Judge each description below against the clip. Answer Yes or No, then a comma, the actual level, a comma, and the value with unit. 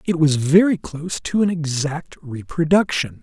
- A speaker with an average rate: Yes, average, 150 wpm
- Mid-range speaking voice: Yes, medium, 160 Hz